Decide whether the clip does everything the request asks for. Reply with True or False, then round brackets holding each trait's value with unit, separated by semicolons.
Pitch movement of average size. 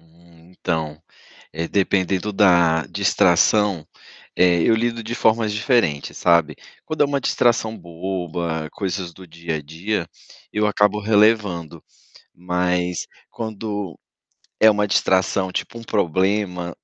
True (3.7 semitones)